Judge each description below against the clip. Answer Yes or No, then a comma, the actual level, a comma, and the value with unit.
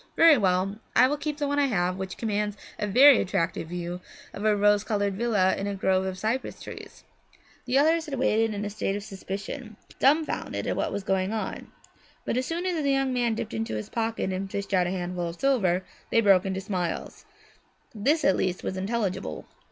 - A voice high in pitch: Yes, high, 205 Hz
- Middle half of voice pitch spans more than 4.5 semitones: Yes, average, 4.9 semitones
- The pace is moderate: No, fast, 210 wpm